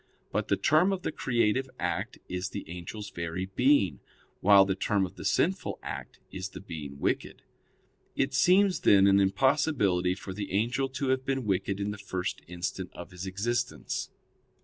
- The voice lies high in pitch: No, low, 100 Hz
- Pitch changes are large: Yes, wide, 6.0 semitones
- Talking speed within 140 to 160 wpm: No, average, 170 wpm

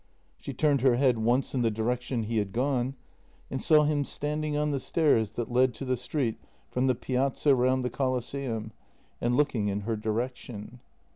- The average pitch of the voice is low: Yes, low, 125 Hz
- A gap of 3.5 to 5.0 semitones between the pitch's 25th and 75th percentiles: No, average, 3.1 semitones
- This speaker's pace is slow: No, average, 185 wpm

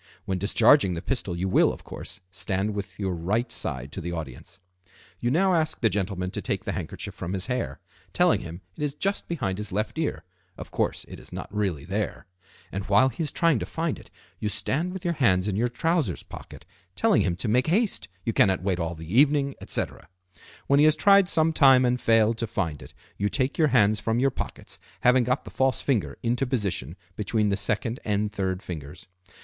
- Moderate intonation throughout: No, wide, 6.3 semitones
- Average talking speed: No, fast, 210 wpm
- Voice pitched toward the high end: No, low, 110 Hz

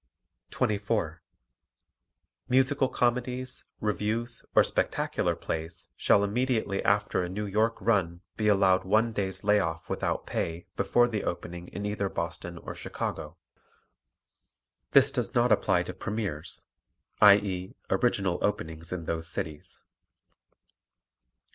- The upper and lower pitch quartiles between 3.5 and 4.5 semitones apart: Yes, average, 4.0 semitones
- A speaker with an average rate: No, slow, 115 wpm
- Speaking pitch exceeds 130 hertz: No, low, 100 Hz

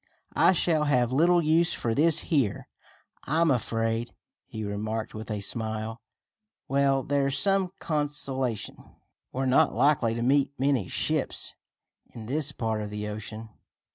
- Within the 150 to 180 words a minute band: No, average, 140 wpm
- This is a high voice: No, low, 130 Hz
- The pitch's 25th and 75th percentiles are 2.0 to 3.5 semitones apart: No, average, 4.8 semitones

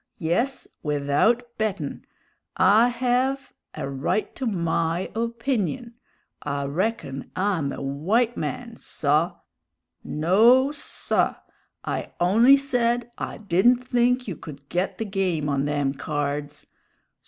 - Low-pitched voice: No, high, 195 Hz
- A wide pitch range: Yes, wide, 8.4 semitones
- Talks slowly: Yes, slow, 115 wpm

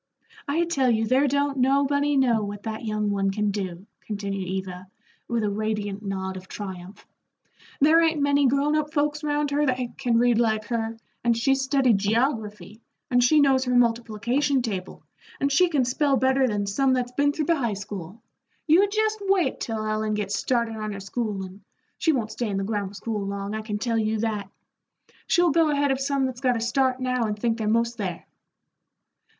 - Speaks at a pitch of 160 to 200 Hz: No, high, 235 Hz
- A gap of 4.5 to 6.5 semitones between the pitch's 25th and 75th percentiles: Yes, average, 4.9 semitones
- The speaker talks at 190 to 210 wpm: Yes, average, 195 wpm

